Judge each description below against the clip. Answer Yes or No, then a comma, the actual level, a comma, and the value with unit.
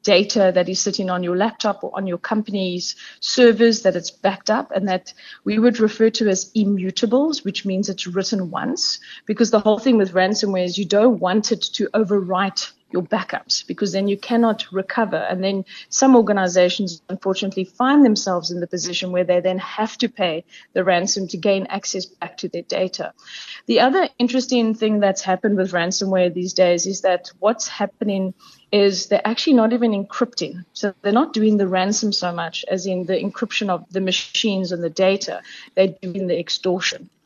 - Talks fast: No, average, 185 wpm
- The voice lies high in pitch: Yes, high, 195 Hz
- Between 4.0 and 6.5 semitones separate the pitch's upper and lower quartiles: No, average, 2.7 semitones